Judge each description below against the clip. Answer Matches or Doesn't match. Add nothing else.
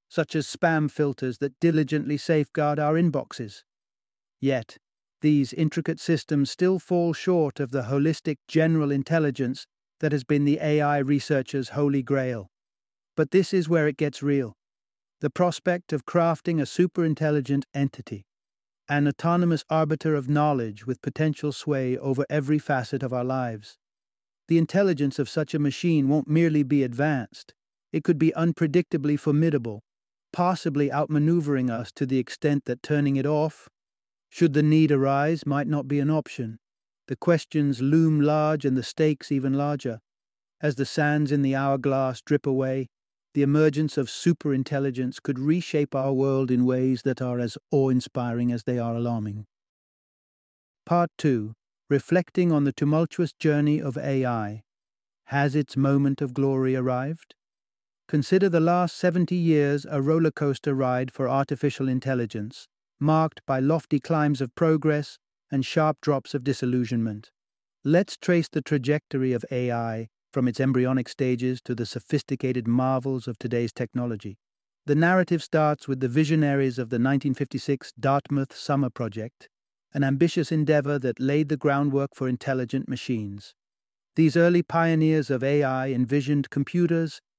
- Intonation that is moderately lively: Matches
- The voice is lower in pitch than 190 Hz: Matches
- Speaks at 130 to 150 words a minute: Matches